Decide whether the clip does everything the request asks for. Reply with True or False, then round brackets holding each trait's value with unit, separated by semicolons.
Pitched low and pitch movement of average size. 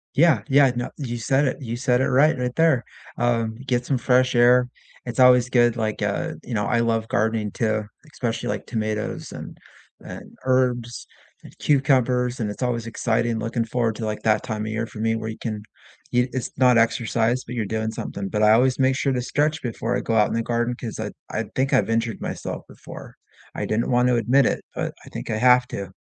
False (120 Hz; 2.2 semitones)